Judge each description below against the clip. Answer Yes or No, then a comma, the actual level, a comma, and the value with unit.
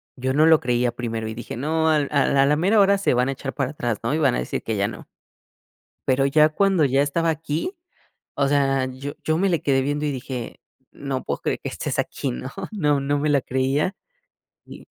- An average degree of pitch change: Yes, average, 3.0 semitones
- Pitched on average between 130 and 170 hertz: Yes, medium, 140 Hz